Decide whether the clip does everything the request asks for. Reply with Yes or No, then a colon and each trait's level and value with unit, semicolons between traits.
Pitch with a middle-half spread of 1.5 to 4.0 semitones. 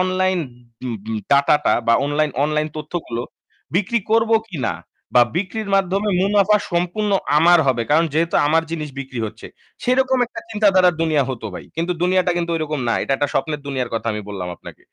No: average, 5.0 semitones